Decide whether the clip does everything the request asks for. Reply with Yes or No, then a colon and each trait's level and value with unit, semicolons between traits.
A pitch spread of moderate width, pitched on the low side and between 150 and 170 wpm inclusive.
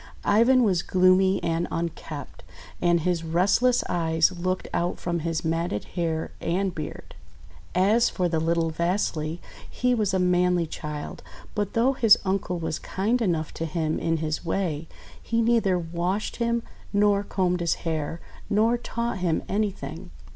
No: average, 3.7 semitones; medium, 180 Hz; average, 155 wpm